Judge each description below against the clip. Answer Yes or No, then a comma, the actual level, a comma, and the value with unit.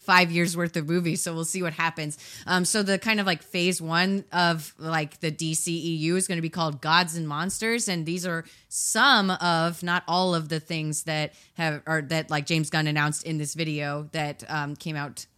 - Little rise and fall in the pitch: Yes, narrow, 2.2 semitones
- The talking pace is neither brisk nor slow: No, fast, 215 wpm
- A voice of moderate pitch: Yes, medium, 165 Hz